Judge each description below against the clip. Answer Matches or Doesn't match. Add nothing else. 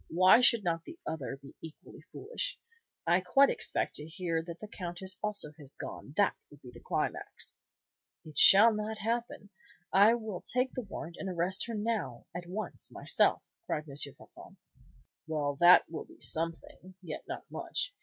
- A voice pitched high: Doesn't match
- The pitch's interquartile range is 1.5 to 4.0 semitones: Doesn't match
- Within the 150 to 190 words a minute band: Matches